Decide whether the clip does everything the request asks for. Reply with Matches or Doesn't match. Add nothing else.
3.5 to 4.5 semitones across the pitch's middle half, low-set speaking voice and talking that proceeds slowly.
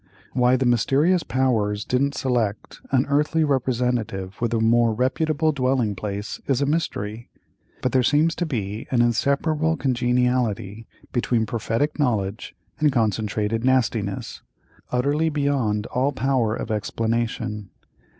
Matches